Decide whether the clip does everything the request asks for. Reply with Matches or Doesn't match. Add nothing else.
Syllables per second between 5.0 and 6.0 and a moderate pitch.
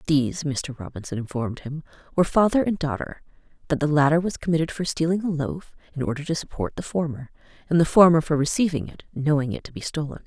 Doesn't match